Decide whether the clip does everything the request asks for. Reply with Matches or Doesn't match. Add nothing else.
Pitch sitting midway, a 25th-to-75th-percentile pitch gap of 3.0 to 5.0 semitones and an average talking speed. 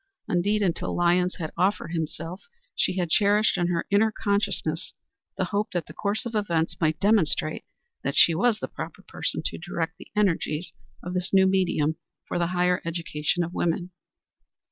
Matches